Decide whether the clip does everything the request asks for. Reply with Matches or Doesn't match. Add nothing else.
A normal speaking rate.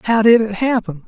Doesn't match